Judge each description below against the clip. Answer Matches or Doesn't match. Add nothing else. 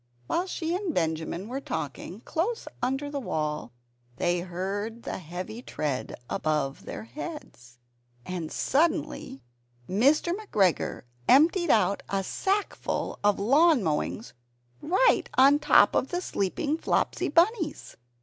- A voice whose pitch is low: Doesn't match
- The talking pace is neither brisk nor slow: Doesn't match